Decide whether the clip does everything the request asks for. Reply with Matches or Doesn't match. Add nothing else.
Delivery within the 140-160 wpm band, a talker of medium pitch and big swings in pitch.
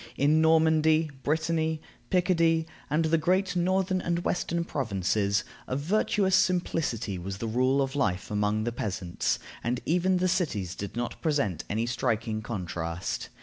Matches